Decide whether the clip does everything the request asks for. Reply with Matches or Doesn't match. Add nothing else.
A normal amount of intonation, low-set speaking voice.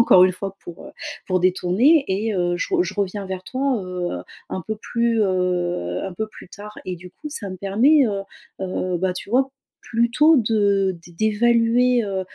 Doesn't match